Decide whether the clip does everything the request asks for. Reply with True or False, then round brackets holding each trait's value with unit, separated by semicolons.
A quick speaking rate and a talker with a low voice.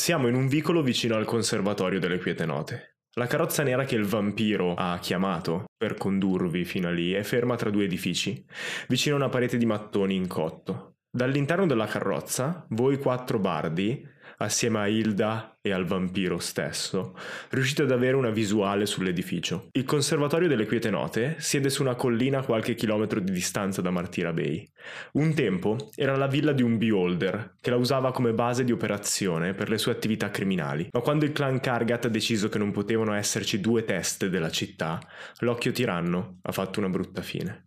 True (180 wpm; 115 Hz)